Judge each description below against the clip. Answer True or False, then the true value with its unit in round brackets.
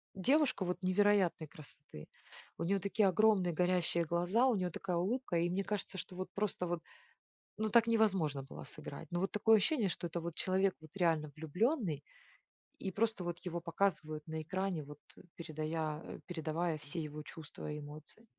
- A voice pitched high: False (175 Hz)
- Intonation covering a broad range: False (4.0 semitones)